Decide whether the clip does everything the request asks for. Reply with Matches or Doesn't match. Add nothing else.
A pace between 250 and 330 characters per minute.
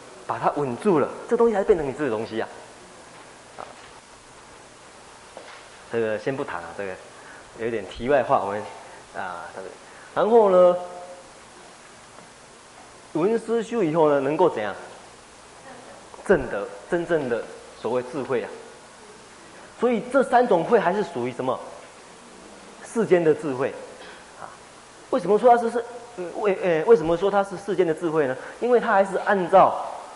Doesn't match